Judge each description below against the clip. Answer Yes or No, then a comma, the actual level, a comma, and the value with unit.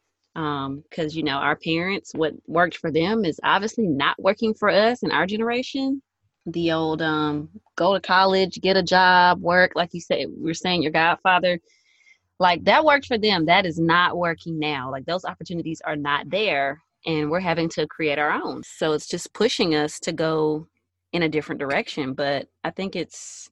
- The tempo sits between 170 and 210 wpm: Yes, average, 190 wpm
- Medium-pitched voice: Yes, medium, 165 Hz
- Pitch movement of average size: Yes, average, 3.6 semitones